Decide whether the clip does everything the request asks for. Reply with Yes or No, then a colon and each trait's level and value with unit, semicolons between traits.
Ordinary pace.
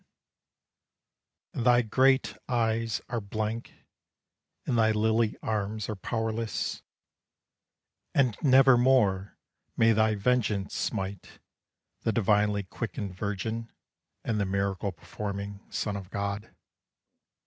No: slow, 100 wpm